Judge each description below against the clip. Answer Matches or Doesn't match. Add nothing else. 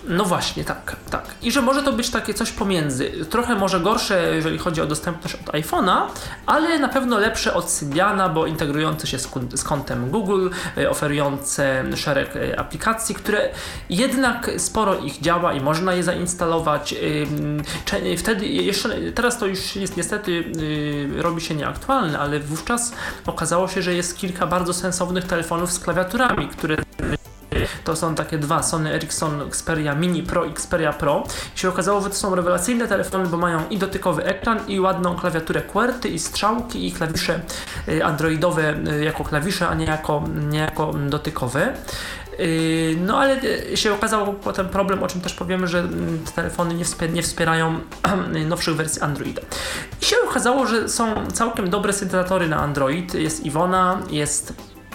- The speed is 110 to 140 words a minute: Doesn't match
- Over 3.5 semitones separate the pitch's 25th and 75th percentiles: Matches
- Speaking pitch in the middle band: Matches